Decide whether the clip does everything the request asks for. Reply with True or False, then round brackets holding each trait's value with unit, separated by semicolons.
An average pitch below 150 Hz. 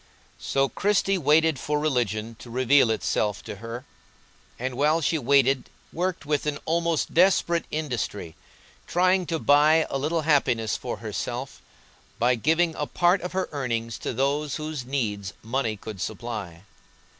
True (140 Hz)